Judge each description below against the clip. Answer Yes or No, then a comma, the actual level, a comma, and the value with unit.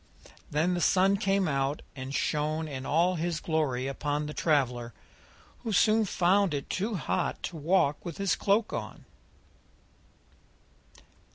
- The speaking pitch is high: No, medium, 160 Hz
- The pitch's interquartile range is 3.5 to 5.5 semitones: Yes, average, 4.7 semitones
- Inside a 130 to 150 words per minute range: Yes, slow, 135 wpm